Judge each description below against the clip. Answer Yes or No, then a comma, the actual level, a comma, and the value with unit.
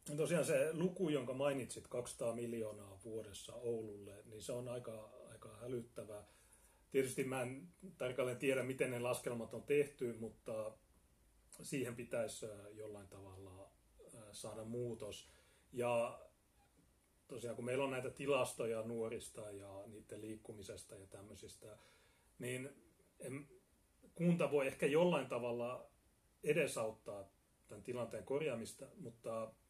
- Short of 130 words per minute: Yes, average, 115 wpm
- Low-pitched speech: Yes, low, 115 Hz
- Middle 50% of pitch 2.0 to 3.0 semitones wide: No, average, 3.4 semitones